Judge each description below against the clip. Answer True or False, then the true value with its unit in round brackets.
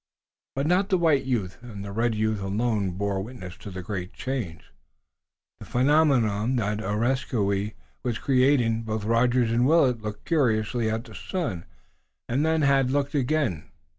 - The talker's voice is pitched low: True (115 Hz)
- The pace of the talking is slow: False (165 wpm)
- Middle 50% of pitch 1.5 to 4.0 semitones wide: False (4.5 semitones)